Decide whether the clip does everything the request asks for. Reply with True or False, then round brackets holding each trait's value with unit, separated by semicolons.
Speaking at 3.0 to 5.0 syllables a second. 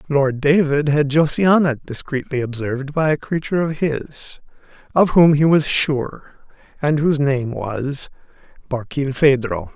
True (4.3 syllables/s)